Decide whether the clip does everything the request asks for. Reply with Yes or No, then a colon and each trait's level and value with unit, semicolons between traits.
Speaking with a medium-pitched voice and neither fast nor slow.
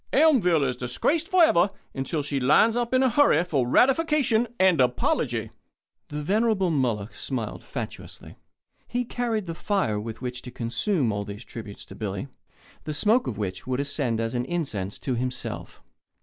Yes: medium, 145 Hz; average, 165 wpm